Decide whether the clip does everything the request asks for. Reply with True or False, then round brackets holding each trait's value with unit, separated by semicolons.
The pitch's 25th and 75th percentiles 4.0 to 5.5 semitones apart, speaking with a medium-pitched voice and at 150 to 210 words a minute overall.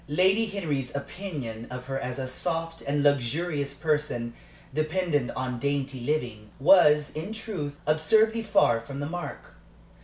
False (4.8 semitones; 145 Hz; 140 wpm)